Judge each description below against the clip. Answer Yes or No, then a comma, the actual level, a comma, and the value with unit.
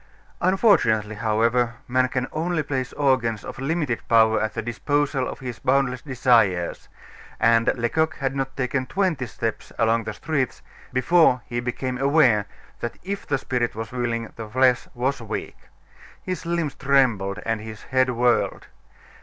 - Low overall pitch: Yes, low, 125 Hz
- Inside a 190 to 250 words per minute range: No, average, 150 wpm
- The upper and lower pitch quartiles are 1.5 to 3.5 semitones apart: Yes, average, 3.2 semitones